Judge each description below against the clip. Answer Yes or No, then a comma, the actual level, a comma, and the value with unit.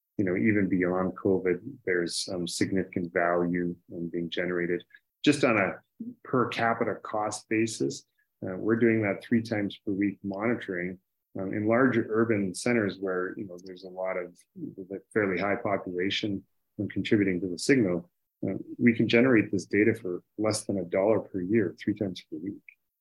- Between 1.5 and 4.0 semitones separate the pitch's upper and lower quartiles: Yes, average, 3.5 semitones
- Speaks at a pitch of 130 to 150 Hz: No, low, 100 Hz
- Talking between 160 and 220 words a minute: Yes, average, 170 wpm